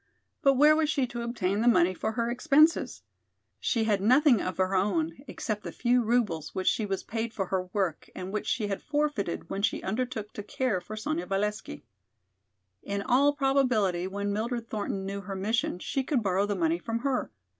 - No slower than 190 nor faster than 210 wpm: Yes, average, 195 wpm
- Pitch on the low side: No, high, 215 Hz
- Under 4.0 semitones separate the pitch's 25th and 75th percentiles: No, average, 4.5 semitones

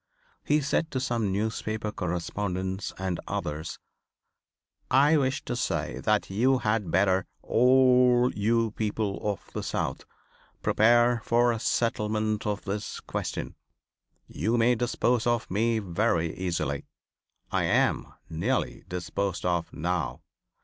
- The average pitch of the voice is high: No, low, 110 Hz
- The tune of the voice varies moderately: Yes, average, 4.3 semitones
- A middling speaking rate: No, slow, 120 wpm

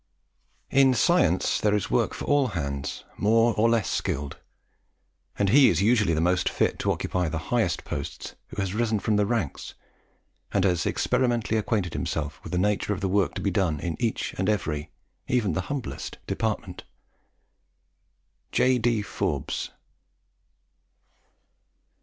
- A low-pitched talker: Yes, low, 105 Hz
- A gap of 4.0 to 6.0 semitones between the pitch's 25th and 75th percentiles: Yes, average, 4.6 semitones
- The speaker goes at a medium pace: Yes, average, 150 wpm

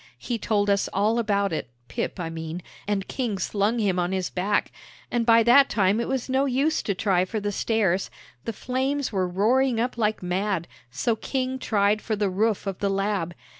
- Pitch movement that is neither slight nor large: Yes, average, 3.7 semitones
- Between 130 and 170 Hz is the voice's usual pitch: No, high, 205 Hz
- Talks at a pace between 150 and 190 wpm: No, average, 200 wpm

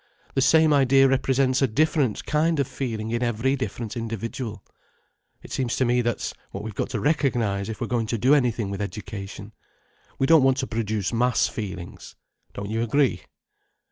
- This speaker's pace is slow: No, average, 175 wpm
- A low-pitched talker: Yes, low, 120 Hz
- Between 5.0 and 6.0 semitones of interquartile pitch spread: No, average, 3.6 semitones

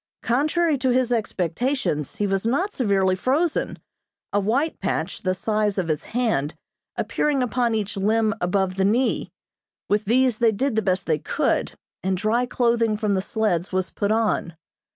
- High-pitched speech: Yes, high, 215 Hz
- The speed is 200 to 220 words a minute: No, average, 165 wpm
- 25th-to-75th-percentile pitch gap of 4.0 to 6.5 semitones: Yes, average, 4.5 semitones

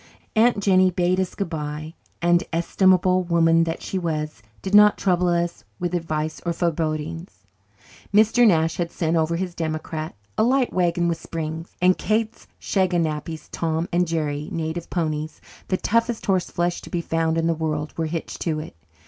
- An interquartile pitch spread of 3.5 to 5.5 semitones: No, narrow, 2.5 semitones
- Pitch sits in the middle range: Yes, medium, 170 Hz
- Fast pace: No, average, 165 wpm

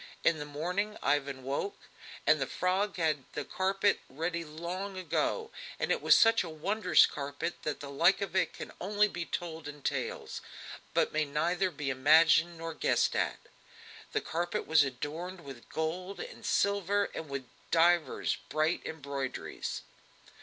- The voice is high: No, medium, 165 Hz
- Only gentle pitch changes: No, average, 4.0 semitones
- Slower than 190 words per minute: Yes, average, 160 wpm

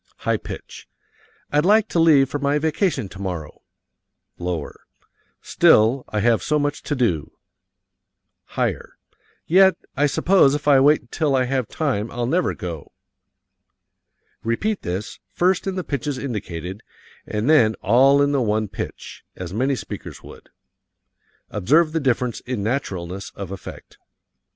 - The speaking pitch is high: No, low, 130 Hz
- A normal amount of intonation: No, wide, 6.2 semitones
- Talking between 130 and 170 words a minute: Yes, average, 140 wpm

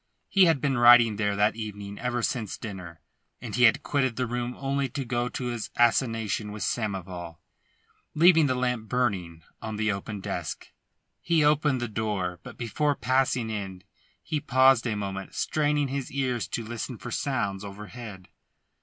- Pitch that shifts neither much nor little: Yes, average, 4.1 semitones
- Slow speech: No, average, 165 wpm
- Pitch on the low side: Yes, low, 120 Hz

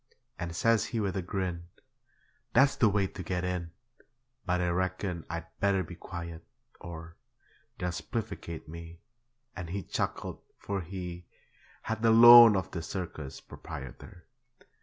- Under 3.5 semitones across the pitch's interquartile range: Yes, average, 2.8 semitones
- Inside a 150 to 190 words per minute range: No, average, 140 wpm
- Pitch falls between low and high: No, very low, 90 Hz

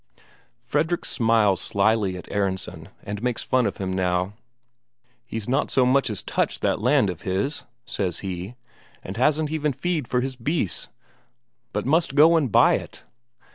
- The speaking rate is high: No, average, 160 wpm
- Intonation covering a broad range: Yes, wide, 6.4 semitones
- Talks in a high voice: No, low, 115 Hz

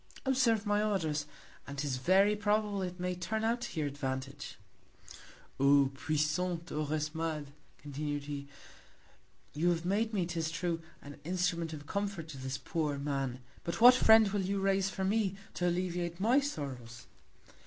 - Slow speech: No, average, 155 wpm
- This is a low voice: No, medium, 170 Hz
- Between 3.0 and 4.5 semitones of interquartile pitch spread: No, average, 5.2 semitones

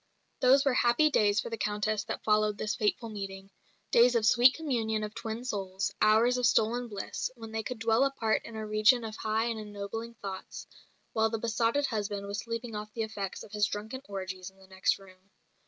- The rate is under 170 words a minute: No, fast, 205 wpm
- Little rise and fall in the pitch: Yes, narrow, 2.3 semitones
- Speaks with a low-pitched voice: No, high, 220 Hz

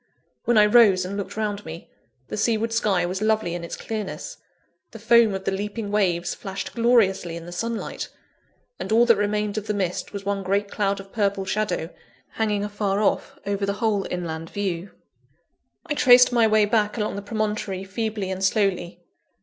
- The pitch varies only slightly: Yes, narrow, 2.1 semitones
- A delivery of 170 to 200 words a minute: Yes, average, 180 wpm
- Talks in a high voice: Yes, high, 205 Hz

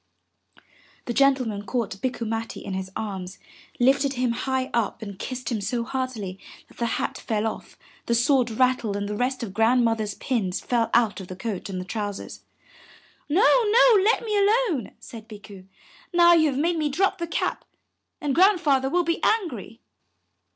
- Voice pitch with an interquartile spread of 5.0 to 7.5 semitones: Yes, wide, 5.4 semitones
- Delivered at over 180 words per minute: No, average, 175 wpm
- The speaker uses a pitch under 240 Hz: No, high, 245 Hz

